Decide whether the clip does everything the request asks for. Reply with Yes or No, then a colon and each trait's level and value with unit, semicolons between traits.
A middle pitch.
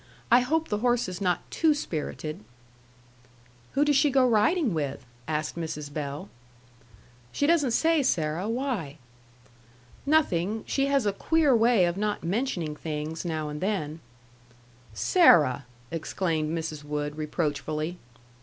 Yes: medium, 180 Hz